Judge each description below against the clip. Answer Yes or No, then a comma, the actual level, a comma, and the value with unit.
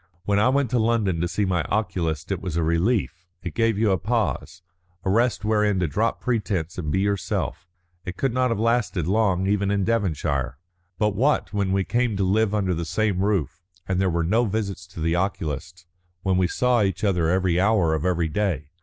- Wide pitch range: No, average, 3.7 semitones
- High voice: No, very low, 95 Hz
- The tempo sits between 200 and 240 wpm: Yes, fast, 205 wpm